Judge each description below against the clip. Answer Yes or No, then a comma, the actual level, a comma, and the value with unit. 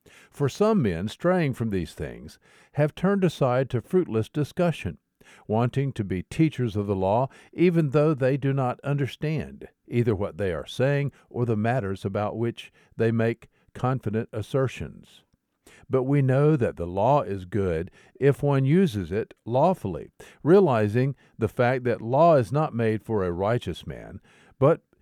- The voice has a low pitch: Yes, low, 125 Hz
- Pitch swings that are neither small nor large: Yes, average, 4.8 semitones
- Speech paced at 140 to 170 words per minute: Yes, average, 160 wpm